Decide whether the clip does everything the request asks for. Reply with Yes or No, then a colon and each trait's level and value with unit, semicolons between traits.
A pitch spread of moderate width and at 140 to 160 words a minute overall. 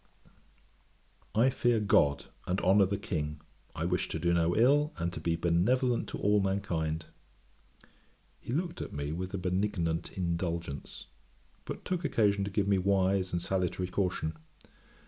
Yes: average, 3.4 semitones; average, 150 wpm